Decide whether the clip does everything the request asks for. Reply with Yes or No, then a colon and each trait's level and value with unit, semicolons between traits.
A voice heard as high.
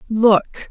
Yes: high, 215 Hz